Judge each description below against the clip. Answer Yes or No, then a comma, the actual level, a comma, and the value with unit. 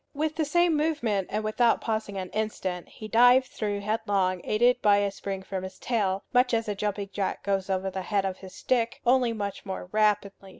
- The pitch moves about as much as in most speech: Yes, average, 3.3 semitones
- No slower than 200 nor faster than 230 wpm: Yes, fast, 205 wpm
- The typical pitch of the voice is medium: No, high, 210 Hz